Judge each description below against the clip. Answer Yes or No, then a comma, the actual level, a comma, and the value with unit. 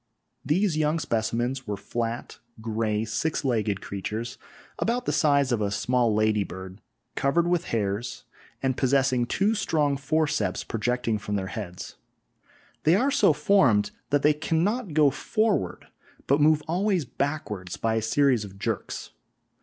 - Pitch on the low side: Yes, low, 130 Hz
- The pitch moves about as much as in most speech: No, wide, 6.2 semitones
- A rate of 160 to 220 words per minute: No, average, 145 wpm